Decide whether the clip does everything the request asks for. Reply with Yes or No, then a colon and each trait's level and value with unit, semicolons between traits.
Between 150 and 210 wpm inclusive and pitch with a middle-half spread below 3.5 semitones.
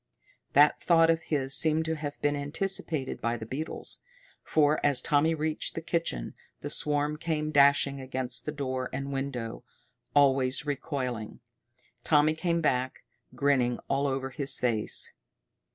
No: slow, 135 wpm; average, 2.8 semitones